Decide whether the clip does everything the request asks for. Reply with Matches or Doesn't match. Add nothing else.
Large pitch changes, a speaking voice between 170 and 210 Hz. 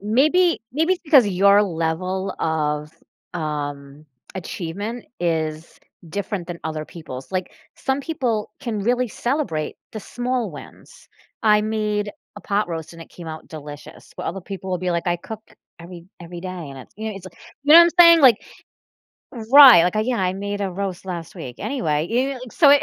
Matches